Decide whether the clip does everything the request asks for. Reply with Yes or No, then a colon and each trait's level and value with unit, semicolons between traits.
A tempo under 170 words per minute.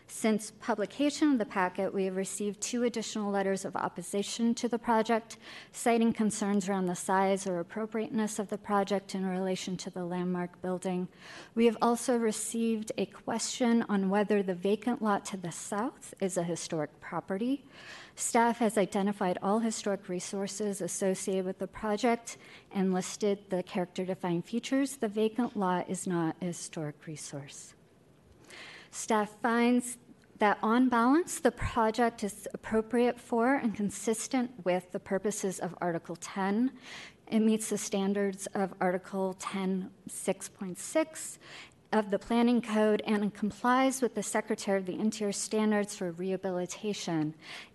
Yes: average, 145 wpm